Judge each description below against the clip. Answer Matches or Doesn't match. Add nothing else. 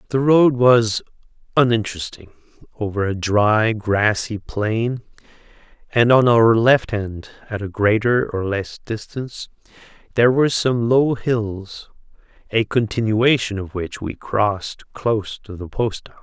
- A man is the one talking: Matches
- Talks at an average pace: Doesn't match